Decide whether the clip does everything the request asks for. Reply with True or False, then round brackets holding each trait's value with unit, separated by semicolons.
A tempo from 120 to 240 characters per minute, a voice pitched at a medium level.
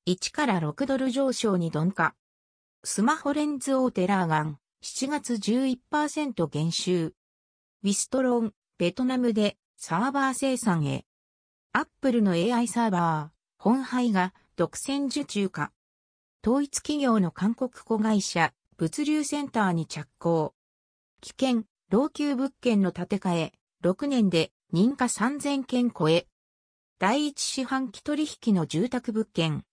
False (225 characters per minute; 205 Hz)